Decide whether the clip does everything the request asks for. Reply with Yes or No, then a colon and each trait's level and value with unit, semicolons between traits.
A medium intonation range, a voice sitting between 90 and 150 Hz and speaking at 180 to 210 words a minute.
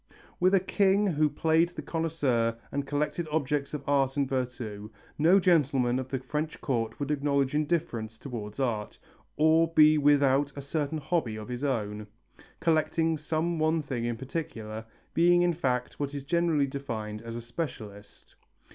No: average, 4.6 semitones; medium, 140 Hz; average, 160 wpm